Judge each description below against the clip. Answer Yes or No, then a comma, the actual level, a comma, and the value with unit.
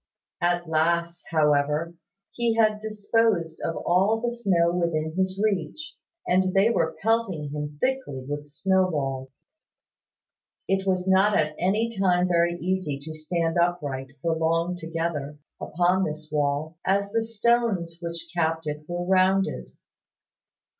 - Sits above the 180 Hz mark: No, medium, 175 Hz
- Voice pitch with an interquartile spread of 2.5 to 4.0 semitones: Yes, average, 3.5 semitones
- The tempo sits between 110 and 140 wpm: Yes, slow, 135 wpm